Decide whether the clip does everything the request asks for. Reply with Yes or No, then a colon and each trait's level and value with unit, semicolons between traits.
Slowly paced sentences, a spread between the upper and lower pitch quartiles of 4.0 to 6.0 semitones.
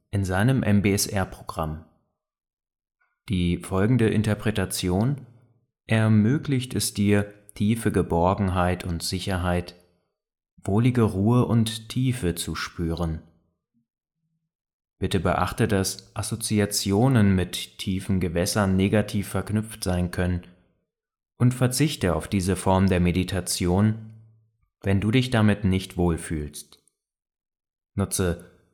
No: slow, 90 wpm; average, 3.6 semitones